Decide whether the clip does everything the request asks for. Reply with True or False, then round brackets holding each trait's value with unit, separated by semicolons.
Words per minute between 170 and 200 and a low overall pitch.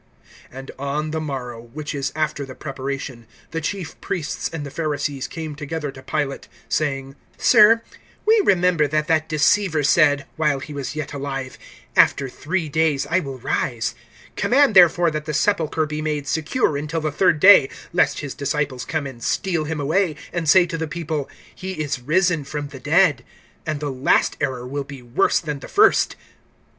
False (175 wpm; 150 Hz)